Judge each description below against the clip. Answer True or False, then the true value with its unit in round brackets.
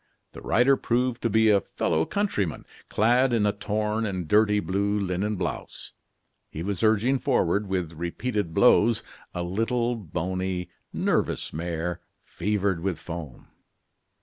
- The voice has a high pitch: False (100 Hz)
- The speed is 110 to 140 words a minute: True (135 wpm)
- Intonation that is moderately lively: True (4.2 semitones)